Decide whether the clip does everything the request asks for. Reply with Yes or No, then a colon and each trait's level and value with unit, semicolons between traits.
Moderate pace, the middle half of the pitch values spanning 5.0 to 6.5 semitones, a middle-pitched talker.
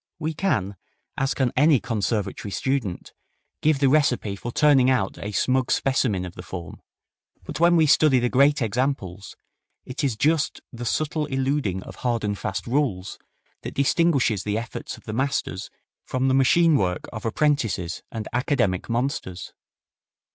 No: average, 155 wpm; wide, 5.5 semitones; low, 125 Hz